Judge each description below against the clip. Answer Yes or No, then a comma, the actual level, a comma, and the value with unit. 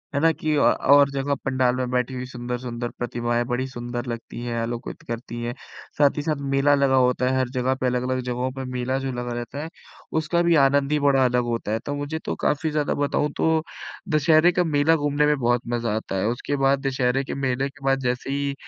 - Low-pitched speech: Yes, low, 130 Hz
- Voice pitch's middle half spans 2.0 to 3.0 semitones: Yes, average, 2.7 semitones